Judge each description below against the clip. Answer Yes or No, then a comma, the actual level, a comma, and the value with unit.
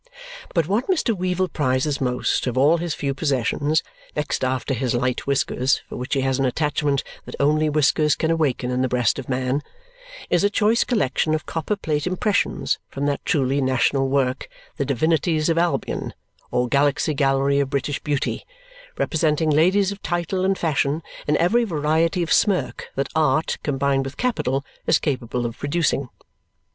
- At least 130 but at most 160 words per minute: No, average, 170 wpm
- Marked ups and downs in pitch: No, average, 3.6 semitones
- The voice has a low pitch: No, medium, 145 Hz